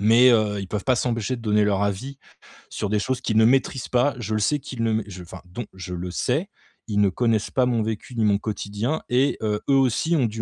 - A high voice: No, low, 110 Hz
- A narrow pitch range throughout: No, average, 3.4 semitones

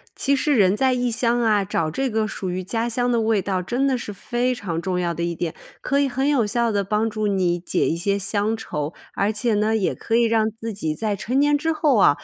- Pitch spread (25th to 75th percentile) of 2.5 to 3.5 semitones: No, average, 4.1 semitones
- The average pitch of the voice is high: Yes, high, 220 Hz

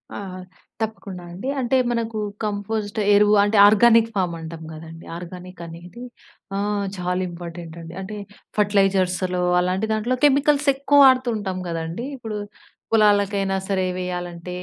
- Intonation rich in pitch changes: No, average, 3.7 semitones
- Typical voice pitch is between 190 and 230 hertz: Yes, high, 200 Hz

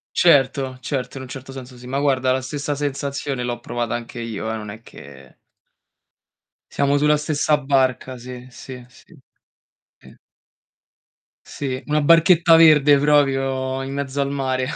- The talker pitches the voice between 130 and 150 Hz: Yes, low, 135 Hz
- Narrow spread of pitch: Yes, narrow, 2.2 semitones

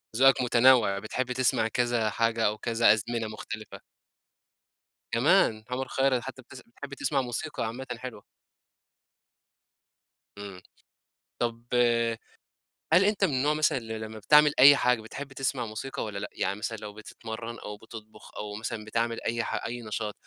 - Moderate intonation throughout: Yes, average, 3.2 semitones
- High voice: No, low, 115 Hz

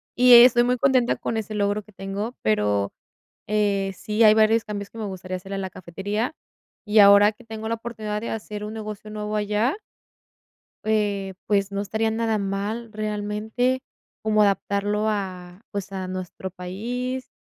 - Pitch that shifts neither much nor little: No, narrow, 2.0 semitones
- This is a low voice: No, high, 210 Hz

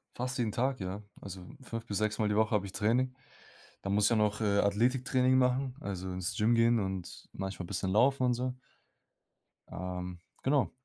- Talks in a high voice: No, low, 105 Hz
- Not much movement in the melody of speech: No, average, 4.4 semitones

